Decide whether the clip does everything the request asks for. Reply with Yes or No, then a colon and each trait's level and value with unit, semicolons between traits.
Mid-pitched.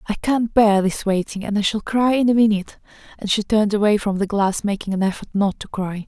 No: high, 205 Hz